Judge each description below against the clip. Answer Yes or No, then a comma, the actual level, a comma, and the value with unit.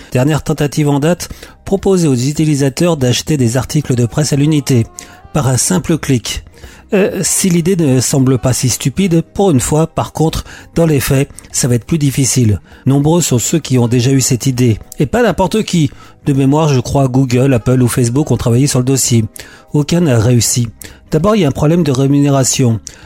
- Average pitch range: Yes, average, 3.9 semitones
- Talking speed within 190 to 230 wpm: Yes, average, 200 wpm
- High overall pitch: No, low, 135 Hz